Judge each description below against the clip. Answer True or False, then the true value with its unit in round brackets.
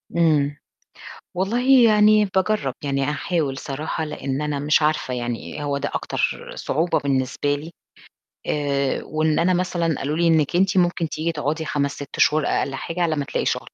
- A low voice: False (155 Hz)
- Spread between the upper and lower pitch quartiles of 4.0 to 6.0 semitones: False (3.5 semitones)